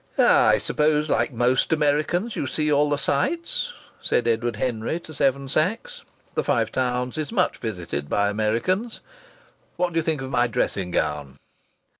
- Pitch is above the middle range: No, medium, 140 Hz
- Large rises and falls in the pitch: Yes, wide, 5.7 semitones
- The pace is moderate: Yes, average, 160 wpm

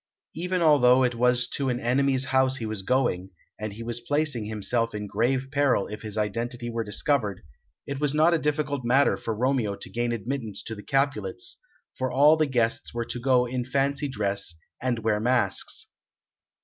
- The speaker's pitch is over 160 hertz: No, low, 125 Hz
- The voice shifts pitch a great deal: No, average, 3.5 semitones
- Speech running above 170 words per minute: Yes, average, 185 wpm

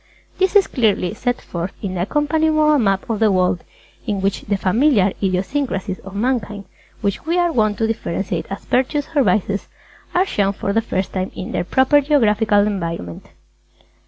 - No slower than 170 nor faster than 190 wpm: Yes, average, 175 wpm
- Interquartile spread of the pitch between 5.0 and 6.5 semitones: Yes, wide, 5.6 semitones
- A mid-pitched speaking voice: No, high, 210 Hz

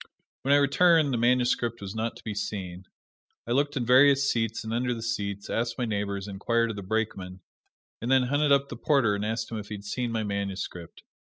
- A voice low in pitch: Yes, low, 115 Hz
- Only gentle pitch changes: No, average, 3.8 semitones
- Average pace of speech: No, fast, 220 wpm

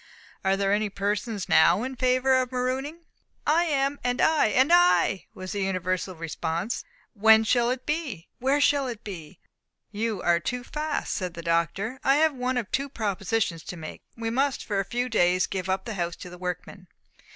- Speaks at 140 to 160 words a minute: No, average, 190 wpm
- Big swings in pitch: Yes, wide, 5.9 semitones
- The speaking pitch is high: Yes, high, 220 Hz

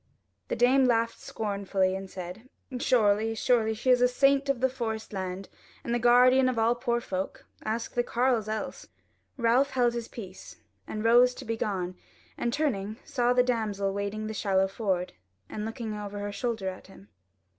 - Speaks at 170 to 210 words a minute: Yes, average, 175 wpm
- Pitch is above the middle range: Yes, high, 225 Hz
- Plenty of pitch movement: No, average, 3.4 semitones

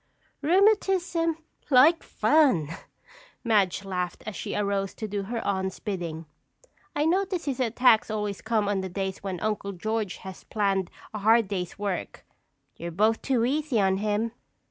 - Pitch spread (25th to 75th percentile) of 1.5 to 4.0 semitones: No, average, 4.8 semitones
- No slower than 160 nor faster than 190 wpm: No, average, 150 wpm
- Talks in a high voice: Yes, high, 210 Hz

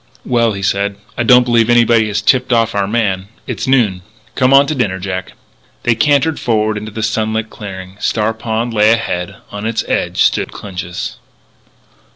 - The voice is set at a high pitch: No, low, 110 Hz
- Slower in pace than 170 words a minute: No, average, 175 wpm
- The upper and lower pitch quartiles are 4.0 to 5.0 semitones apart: No, average, 2.8 semitones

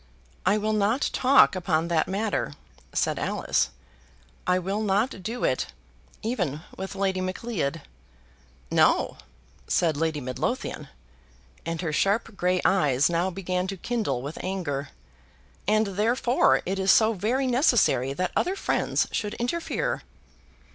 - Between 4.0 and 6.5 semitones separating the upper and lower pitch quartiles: Yes, average, 4.7 semitones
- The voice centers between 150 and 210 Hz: Yes, high, 190 Hz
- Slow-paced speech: Yes, slow, 130 wpm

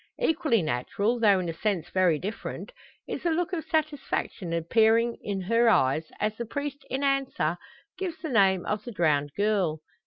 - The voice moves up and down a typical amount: No, wide, 7.7 semitones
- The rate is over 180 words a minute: No, average, 175 wpm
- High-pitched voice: Yes, high, 215 Hz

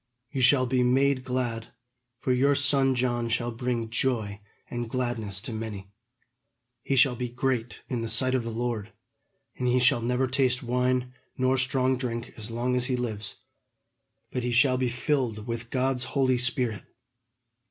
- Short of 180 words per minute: Yes, average, 165 wpm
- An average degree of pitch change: No, narrow, 1.8 semitones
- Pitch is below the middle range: Yes, low, 125 Hz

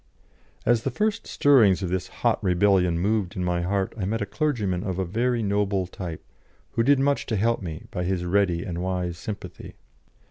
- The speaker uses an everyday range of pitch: Yes, average, 4.0 semitones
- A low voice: Yes, very low, 95 Hz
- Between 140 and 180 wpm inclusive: No, average, 190 wpm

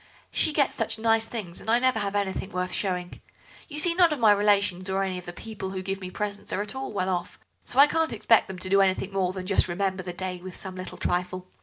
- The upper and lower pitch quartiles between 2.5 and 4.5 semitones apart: Yes, average, 3.2 semitones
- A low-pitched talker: No, high, 195 Hz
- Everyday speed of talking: No, fast, 260 wpm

